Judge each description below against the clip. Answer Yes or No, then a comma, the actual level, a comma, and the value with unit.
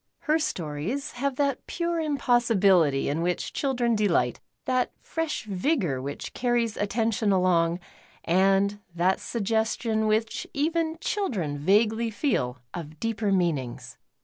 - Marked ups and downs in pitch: Yes, wide, 6.2 semitones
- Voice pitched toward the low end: No, high, 215 Hz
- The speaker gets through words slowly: Yes, slow, 120 wpm